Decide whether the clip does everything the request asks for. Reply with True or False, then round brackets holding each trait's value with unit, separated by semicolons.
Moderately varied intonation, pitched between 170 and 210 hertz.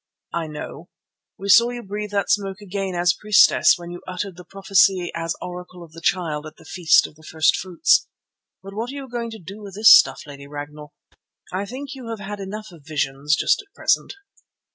True (4.0 semitones; 190 Hz)